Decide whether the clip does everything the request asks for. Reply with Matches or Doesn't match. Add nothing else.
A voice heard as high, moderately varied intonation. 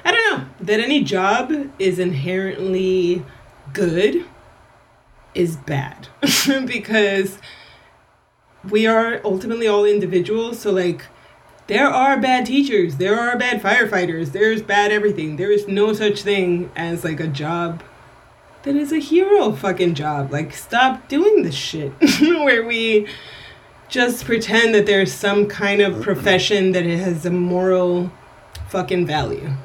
Matches